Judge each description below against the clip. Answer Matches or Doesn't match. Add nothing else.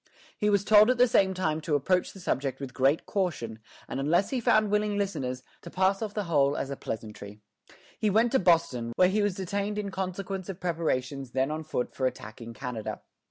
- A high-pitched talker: Doesn't match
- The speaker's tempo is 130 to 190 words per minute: Doesn't match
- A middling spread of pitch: Doesn't match